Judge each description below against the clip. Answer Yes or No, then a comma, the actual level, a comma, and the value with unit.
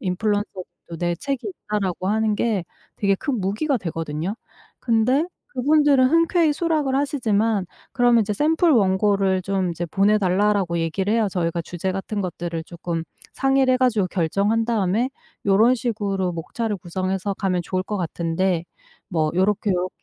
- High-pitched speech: Yes, high, 200 Hz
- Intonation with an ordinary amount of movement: Yes, average, 4.5 semitones